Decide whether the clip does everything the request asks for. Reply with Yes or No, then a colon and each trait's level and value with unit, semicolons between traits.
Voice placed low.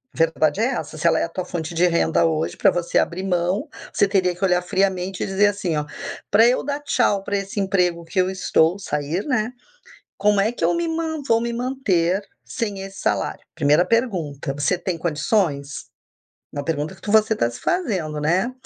No: medium, 185 Hz